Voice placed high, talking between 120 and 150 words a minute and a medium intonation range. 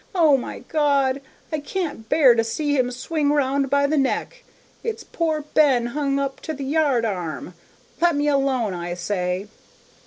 No: very high, 275 Hz; average, 165 wpm; average, 3.9 semitones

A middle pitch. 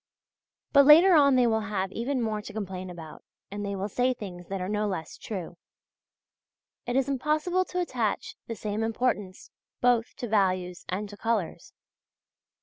No: high, 215 Hz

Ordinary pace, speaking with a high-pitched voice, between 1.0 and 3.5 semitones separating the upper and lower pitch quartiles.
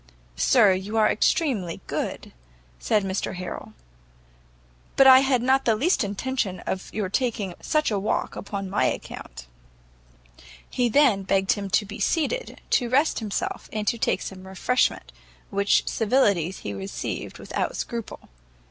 No: average, 145 wpm; high, 210 Hz; average, 4.8 semitones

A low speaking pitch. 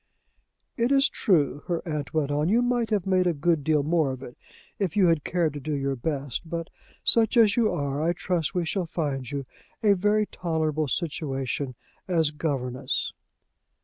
No: medium, 160 Hz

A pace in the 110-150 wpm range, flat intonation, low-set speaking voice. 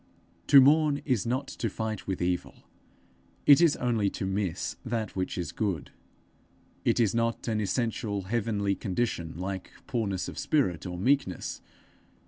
No: average, 145 wpm; average, 4.3 semitones; low, 110 Hz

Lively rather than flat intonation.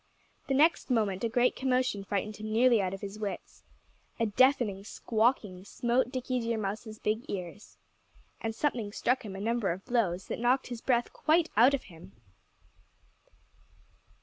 No: average, 3.8 semitones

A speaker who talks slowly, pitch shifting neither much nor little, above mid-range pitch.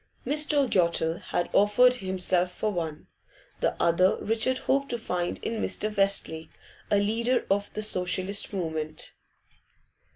Yes: slow, 130 wpm; average, 4.2 semitones; high, 200 Hz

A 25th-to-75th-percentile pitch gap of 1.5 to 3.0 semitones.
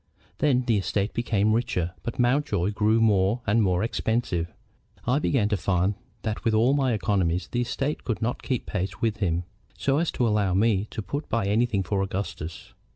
No: average, 3.7 semitones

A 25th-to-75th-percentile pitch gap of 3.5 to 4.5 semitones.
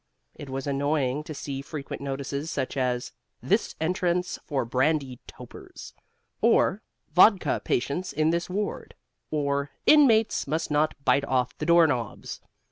Yes: average, 3.8 semitones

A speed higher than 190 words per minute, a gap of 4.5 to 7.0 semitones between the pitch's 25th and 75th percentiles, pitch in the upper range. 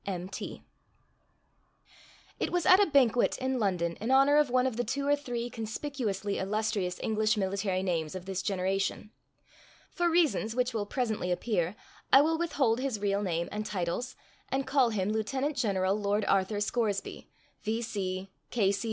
No: average, 150 wpm; average, 5.0 semitones; high, 215 Hz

